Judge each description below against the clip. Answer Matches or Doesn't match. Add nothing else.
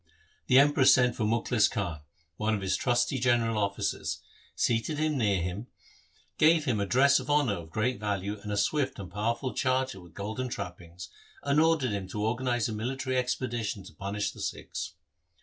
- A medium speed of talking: Matches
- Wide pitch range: Doesn't match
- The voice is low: Matches